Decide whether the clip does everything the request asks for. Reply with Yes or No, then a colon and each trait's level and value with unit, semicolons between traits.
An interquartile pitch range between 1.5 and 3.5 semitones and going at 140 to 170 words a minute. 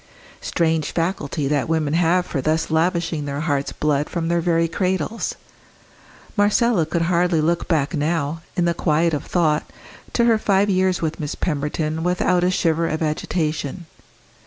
Yes: narrow, 2.6 semitones; average, 160 wpm